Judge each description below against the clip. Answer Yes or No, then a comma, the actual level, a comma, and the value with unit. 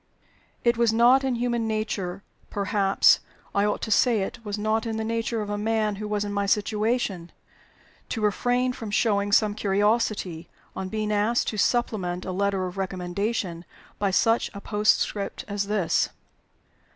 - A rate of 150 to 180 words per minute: Yes, average, 165 wpm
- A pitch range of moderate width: No, narrow, 2.2 semitones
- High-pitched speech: Yes, high, 210 Hz